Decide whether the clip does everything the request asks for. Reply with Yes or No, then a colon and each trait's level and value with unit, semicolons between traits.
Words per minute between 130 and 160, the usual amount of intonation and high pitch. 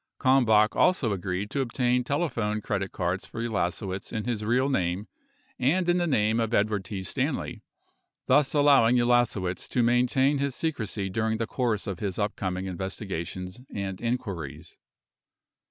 No: average, 155 wpm; average, 4.5 semitones; low, 110 Hz